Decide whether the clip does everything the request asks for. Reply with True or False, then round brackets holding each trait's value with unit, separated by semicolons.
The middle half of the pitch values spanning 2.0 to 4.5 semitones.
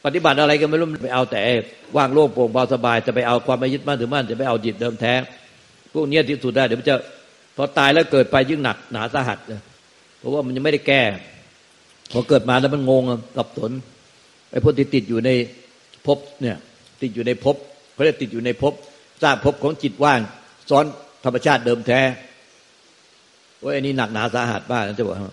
True (2.8 semitones)